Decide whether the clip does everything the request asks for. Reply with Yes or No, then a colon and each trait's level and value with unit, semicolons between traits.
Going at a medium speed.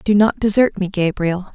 Yes: average, 195 wpm